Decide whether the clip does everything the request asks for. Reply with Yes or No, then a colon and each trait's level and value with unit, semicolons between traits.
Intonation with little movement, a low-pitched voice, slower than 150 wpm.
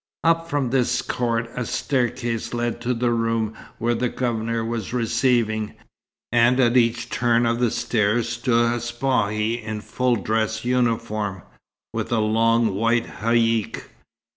Yes: narrow, 1.2 semitones; low, 115 Hz; average, 140 wpm